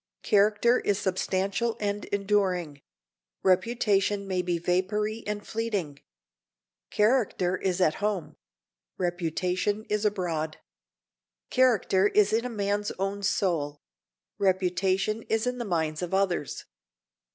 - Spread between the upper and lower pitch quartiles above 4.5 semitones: No, average, 2.7 semitones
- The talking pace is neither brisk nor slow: No, slow, 110 wpm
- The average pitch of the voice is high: Yes, high, 195 Hz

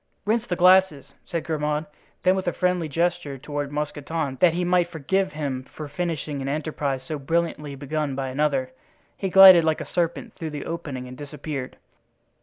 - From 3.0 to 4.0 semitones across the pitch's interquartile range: Yes, average, 3.6 semitones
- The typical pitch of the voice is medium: Yes, medium, 155 Hz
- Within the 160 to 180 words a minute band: Yes, average, 175 wpm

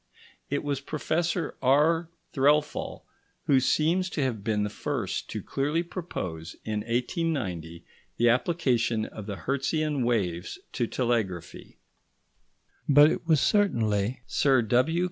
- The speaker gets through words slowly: Yes, slow, 125 wpm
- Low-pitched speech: Yes, low, 130 Hz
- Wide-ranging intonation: Yes, wide, 5.9 semitones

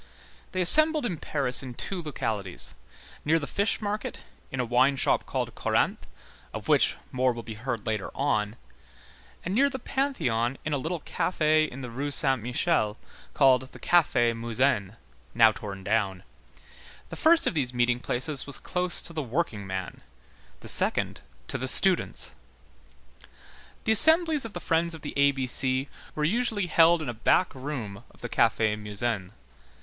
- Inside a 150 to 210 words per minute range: Yes, average, 165 wpm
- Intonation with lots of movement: Yes, wide, 6.7 semitones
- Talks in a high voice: No, low, 135 Hz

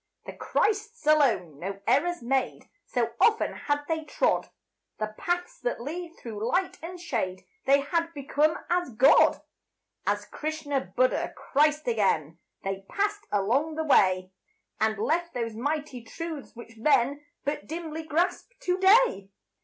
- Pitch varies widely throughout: Yes, wide, 6.9 semitones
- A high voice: Yes, very high, 290 Hz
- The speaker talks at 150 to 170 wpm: No, average, 140 wpm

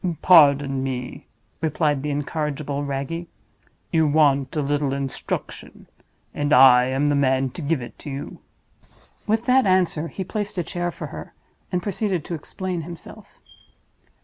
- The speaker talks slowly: No, average, 145 wpm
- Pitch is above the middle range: No, medium, 150 Hz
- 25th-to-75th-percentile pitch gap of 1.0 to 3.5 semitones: No, average, 4.0 semitones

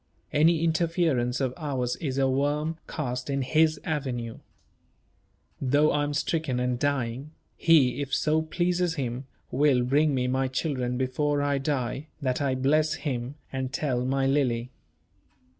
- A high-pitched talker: No, medium, 140 Hz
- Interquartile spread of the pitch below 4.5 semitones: Yes, average, 3.2 semitones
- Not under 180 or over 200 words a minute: No, average, 150 wpm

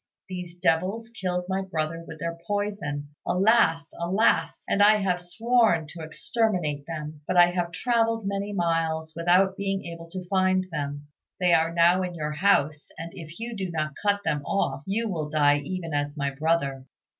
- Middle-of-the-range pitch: Yes, medium, 175 Hz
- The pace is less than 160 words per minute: No, average, 175 wpm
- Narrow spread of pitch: No, average, 3.7 semitones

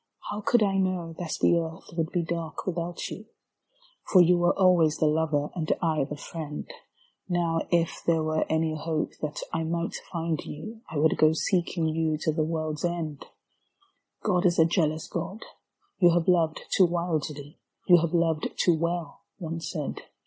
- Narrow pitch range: Yes, narrow, 1.8 semitones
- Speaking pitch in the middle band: Yes, medium, 165 Hz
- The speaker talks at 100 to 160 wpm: No, average, 175 wpm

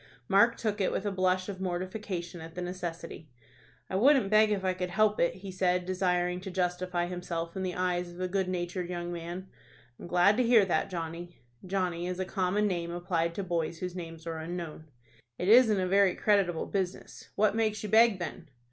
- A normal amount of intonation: No, narrow, 2.0 semitones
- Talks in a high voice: No, medium, 180 Hz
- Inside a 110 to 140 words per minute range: No, average, 200 wpm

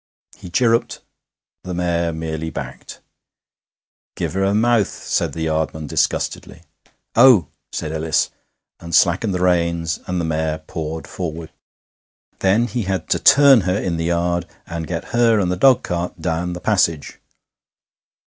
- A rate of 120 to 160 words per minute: Yes, average, 145 wpm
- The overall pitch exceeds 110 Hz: No, very low, 85 Hz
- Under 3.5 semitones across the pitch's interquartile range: Yes, average, 3.0 semitones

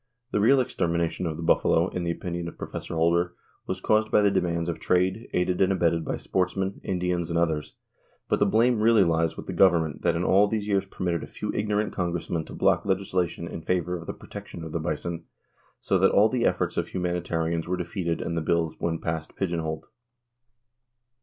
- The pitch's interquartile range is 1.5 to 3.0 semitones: Yes, narrow, 2.5 semitones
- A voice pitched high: No, very low, 90 Hz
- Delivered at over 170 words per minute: Yes, fast, 205 wpm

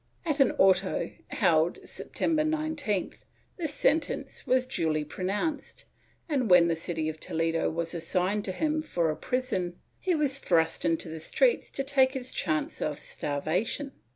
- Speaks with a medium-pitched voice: No, high, 195 Hz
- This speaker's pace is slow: No, average, 155 wpm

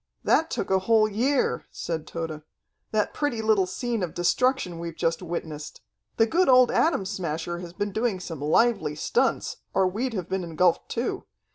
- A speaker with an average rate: Yes, average, 170 wpm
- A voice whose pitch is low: No, high, 190 Hz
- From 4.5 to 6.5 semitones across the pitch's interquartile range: Yes, wide, 5.6 semitones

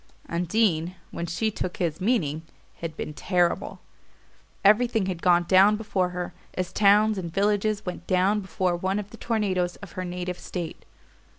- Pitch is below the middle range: No, medium, 185 Hz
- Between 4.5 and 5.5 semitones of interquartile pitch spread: No, average, 3.0 semitones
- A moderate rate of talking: Yes, average, 160 wpm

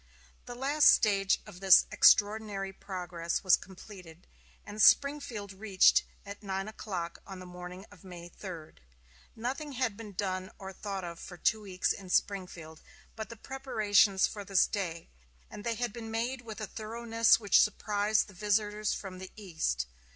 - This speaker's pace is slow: No, average, 160 wpm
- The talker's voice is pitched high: Yes, high, 200 Hz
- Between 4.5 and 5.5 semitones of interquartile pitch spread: No, average, 2.9 semitones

